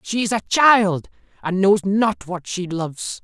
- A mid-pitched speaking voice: Yes, medium, 180 Hz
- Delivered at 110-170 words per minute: No, average, 185 wpm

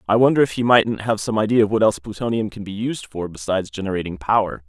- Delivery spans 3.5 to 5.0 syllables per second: No, 6.7 syllables/s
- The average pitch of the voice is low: Yes, low, 105 Hz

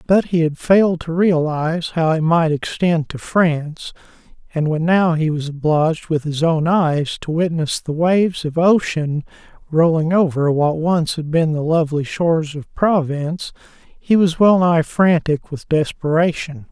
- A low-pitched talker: No, medium, 160 Hz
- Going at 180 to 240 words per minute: No, average, 165 wpm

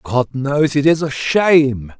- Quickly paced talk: No, average, 180 wpm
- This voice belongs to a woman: No, male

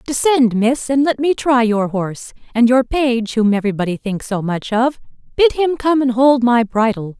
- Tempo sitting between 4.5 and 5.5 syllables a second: Yes, 4.8 syllables/s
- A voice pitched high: Yes, high, 245 Hz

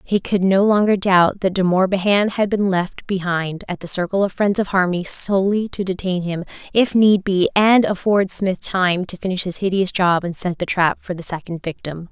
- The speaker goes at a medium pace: No, fast, 215 wpm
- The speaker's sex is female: Yes, female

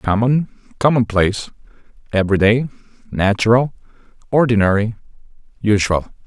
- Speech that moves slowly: Yes, slow, 55 wpm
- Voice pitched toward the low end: Yes, low, 110 Hz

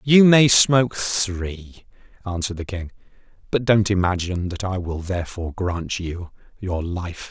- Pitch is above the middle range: No, very low, 95 Hz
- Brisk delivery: No, average, 150 wpm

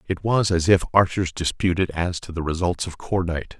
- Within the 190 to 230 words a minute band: Yes, average, 200 wpm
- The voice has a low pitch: Yes, very low, 90 Hz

